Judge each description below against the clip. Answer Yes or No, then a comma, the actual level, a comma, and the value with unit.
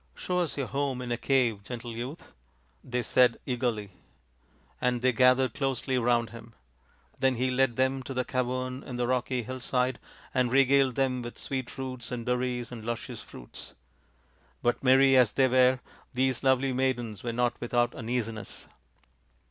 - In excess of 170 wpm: No, average, 165 wpm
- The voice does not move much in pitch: Yes, narrow, 1.5 semitones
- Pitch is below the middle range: Yes, low, 125 Hz